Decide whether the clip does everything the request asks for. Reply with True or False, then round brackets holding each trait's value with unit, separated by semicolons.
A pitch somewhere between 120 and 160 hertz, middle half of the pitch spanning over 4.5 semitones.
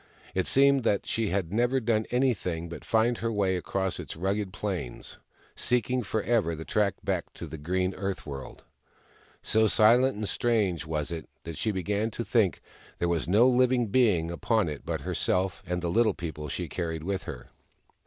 False (100 Hz; 5.1 semitones)